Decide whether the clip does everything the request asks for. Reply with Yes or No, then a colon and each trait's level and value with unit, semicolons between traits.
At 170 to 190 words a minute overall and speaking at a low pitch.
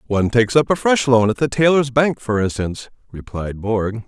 No: fast, 205 wpm; low, 120 Hz